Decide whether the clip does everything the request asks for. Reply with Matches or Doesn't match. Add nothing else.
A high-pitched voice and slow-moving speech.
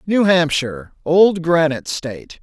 Doesn't match